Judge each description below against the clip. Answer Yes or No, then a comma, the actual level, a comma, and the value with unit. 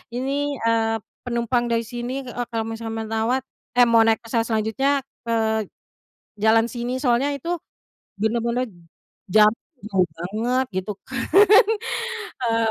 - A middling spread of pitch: No, narrow, 1.8 semitones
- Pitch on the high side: Yes, high, 230 Hz